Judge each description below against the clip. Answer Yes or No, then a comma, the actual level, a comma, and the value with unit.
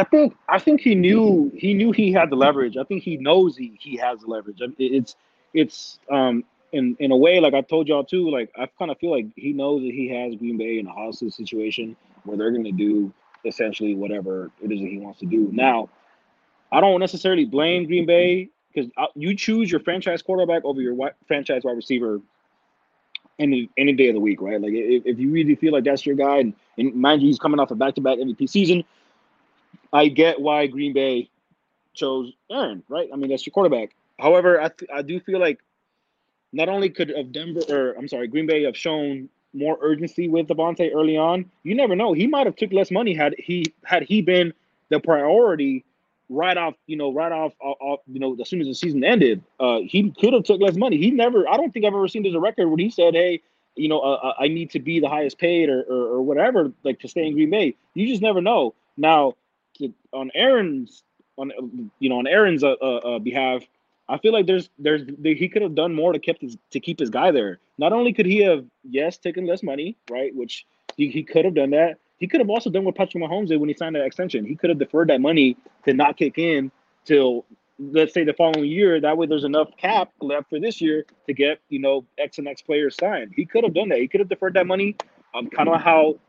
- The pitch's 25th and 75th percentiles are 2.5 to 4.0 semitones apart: No, average, 5.3 semitones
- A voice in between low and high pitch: Yes, medium, 155 Hz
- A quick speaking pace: Yes, fast, 235 wpm